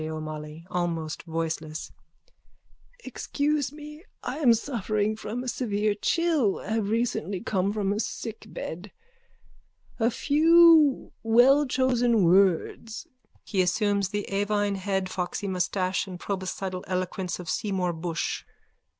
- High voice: Yes, high, 205 Hz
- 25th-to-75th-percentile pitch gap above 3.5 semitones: Yes, average, 4.6 semitones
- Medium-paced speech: No, slow, 110 wpm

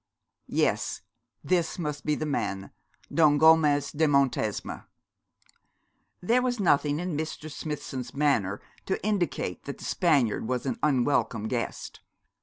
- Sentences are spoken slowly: Yes, slow, 125 wpm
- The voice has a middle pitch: Yes, medium, 150 Hz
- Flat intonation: No, average, 4.1 semitones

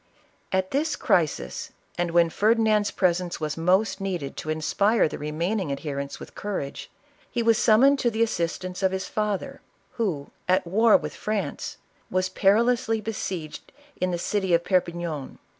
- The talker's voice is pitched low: No, medium, 185 Hz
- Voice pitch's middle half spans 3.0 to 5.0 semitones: Yes, average, 4.3 semitones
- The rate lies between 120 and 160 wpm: Yes, average, 155 wpm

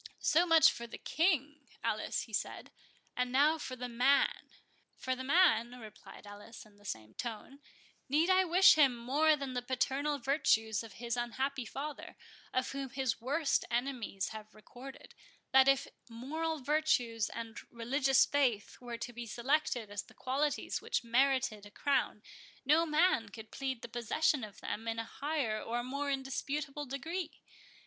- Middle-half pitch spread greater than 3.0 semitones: Yes, average, 3.8 semitones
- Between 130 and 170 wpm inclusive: Yes, average, 160 wpm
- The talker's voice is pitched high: Yes, very high, 260 Hz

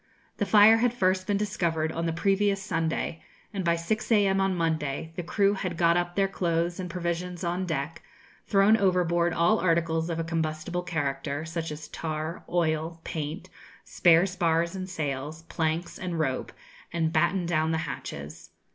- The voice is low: No, medium, 170 Hz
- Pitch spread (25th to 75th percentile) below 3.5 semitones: Yes, narrow, 2.5 semitones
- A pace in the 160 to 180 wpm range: Yes, average, 165 wpm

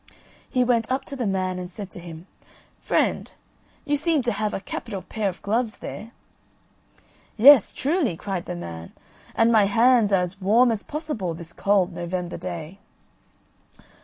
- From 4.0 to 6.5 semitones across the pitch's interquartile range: Yes, average, 5.1 semitones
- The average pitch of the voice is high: Yes, high, 205 Hz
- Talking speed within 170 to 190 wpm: No, average, 160 wpm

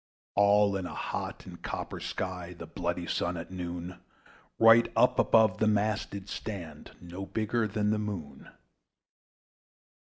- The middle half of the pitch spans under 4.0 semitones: Yes, average, 3.4 semitones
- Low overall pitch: Yes, very low, 95 Hz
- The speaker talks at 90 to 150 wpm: Yes, average, 140 wpm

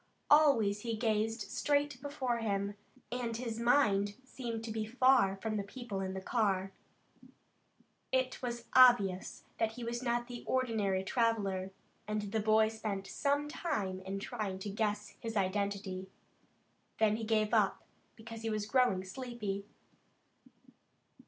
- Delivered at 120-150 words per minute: Yes, average, 145 wpm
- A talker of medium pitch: No, high, 220 Hz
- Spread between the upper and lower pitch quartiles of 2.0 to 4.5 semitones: Yes, average, 3.4 semitones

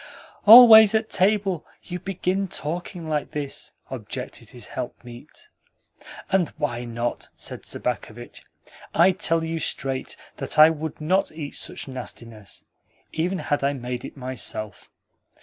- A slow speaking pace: Yes, slow, 130 wpm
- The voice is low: No, medium, 155 Hz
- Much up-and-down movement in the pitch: Yes, wide, 6.5 semitones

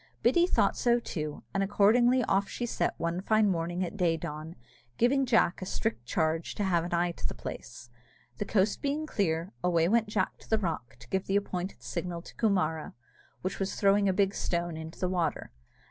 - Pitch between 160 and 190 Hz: Yes, medium, 185 Hz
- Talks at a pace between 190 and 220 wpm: Yes, average, 200 wpm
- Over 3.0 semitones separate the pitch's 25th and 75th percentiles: Yes, average, 3.9 semitones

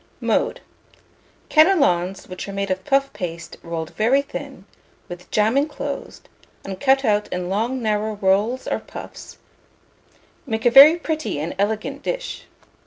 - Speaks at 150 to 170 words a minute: No, average, 140 wpm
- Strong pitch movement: Yes, wide, 6.4 semitones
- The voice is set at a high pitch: Yes, high, 215 Hz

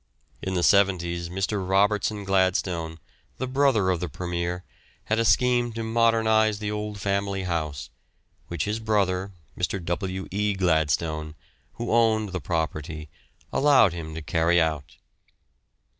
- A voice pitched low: Yes, very low, 95 Hz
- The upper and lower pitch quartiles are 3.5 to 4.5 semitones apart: Yes, average, 3.8 semitones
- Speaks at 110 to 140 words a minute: Yes, slow, 135 wpm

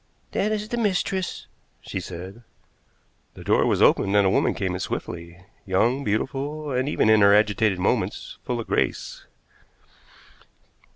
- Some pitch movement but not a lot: No, wide, 7.1 semitones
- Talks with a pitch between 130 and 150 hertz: No, low, 110 Hz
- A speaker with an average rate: Yes, average, 150 wpm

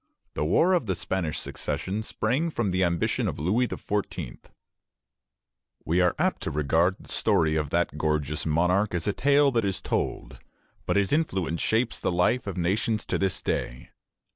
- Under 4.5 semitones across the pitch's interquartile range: No, average, 4.9 semitones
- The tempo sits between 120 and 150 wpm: No, average, 170 wpm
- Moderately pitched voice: No, very low, 95 Hz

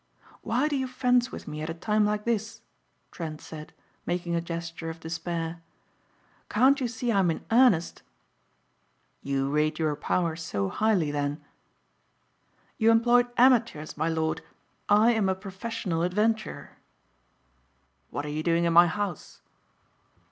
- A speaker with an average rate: Yes, average, 145 wpm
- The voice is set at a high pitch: No, medium, 175 Hz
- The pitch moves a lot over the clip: Yes, wide, 5.8 semitones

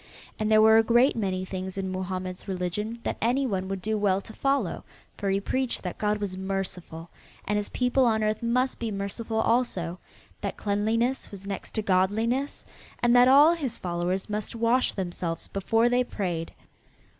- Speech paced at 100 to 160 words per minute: No, average, 180 wpm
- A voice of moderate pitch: No, high, 210 Hz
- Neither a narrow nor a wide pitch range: Yes, average, 3.8 semitones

